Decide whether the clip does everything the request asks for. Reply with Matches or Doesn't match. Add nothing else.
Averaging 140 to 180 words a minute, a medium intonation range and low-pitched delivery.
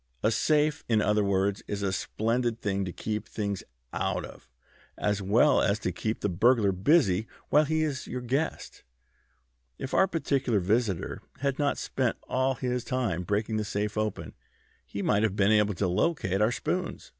Matches